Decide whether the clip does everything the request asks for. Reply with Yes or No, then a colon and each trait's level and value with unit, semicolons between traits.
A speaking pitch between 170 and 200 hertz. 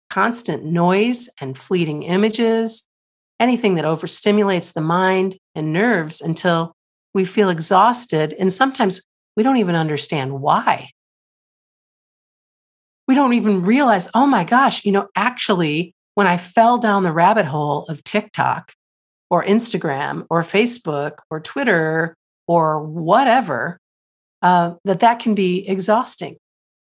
Yes: high, 190 Hz